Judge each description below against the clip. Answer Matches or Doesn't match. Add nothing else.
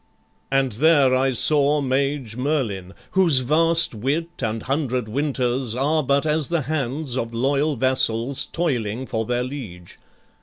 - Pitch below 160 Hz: Matches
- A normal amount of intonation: Matches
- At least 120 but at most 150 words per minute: Matches